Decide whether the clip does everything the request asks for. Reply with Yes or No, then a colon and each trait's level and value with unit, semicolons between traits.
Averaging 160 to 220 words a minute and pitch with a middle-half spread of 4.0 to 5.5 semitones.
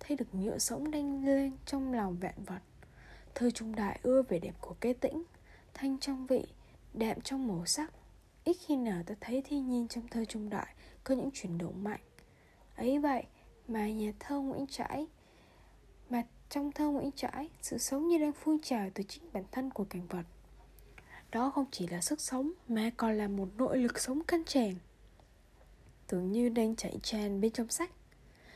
Yes: average, 185 wpm; average, 5.1 semitones